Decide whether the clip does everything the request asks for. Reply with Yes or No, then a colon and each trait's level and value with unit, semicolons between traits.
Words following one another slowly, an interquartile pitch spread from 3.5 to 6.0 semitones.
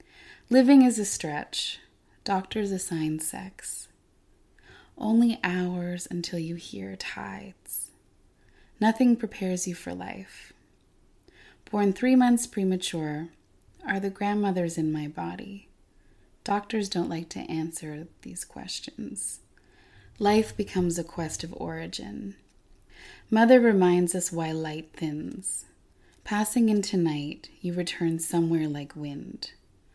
Yes: slow, 110 wpm; wide, 5.4 semitones